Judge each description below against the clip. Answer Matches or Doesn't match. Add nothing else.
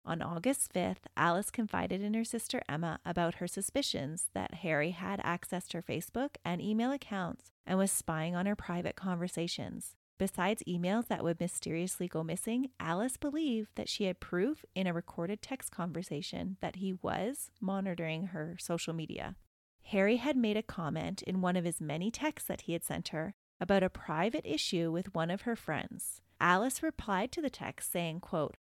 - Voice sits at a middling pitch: Matches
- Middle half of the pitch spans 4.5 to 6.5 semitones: Doesn't match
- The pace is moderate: Matches